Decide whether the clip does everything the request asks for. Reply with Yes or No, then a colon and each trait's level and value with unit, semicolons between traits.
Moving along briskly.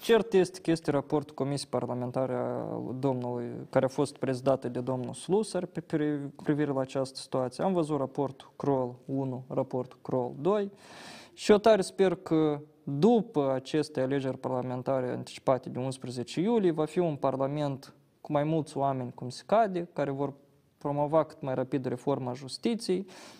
No: average, 155 wpm